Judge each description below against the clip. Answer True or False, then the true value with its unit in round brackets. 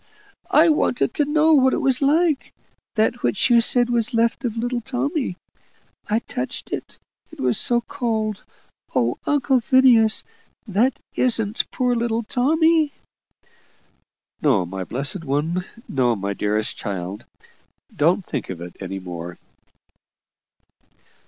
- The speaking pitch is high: True (230 Hz)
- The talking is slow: True (130 wpm)